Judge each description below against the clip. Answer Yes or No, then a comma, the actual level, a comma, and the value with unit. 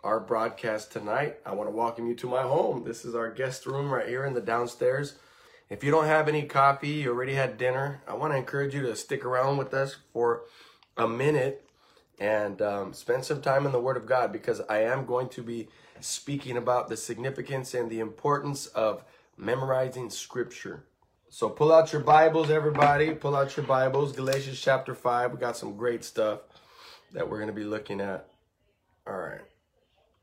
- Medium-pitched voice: No, low, 130 Hz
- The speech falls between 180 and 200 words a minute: Yes, average, 190 wpm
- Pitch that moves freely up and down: No, average, 3.3 semitones